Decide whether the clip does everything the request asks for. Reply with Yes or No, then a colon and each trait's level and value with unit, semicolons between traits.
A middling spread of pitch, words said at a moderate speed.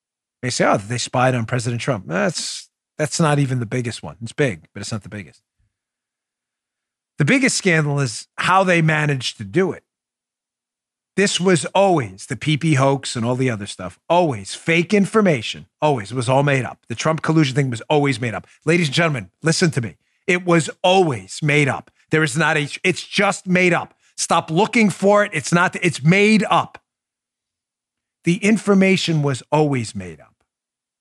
No: wide, 6.1 semitones; average, 180 wpm